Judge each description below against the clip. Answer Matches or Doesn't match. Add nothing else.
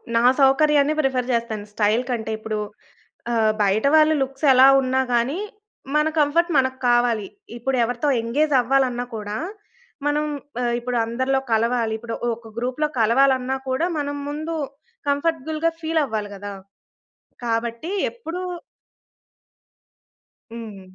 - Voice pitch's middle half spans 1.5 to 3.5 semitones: Doesn't match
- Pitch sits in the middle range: Doesn't match